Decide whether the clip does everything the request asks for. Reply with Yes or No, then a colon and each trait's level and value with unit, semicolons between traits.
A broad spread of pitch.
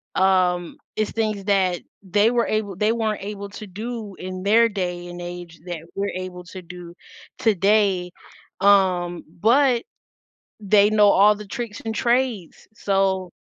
No: average, 2.9 semitones